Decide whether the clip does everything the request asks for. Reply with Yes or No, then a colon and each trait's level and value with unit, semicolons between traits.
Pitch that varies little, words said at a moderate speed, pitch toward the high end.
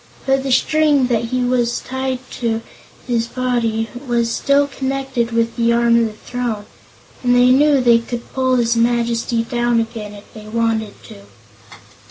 Yes: narrow, 1.8 semitones; average, 160 wpm; high, 235 Hz